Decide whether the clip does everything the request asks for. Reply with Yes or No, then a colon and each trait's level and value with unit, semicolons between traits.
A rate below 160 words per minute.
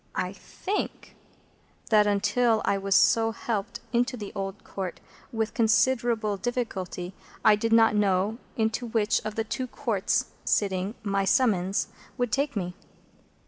Yes: average, 140 wpm